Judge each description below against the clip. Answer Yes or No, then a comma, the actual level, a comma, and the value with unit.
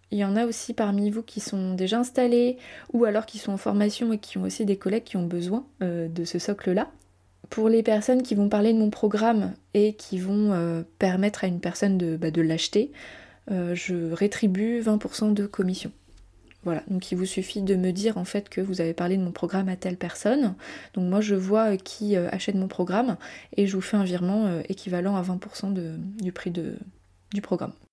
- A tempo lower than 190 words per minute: No, average, 210 wpm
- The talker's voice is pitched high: Yes, high, 195 Hz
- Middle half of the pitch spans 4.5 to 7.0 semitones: No, average, 2.9 semitones